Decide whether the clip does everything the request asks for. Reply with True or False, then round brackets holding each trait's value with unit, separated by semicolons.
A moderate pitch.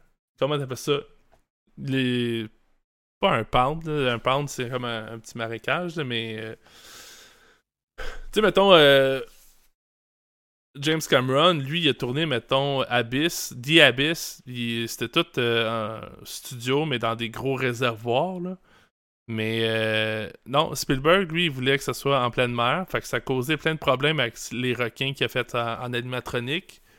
False (130 Hz)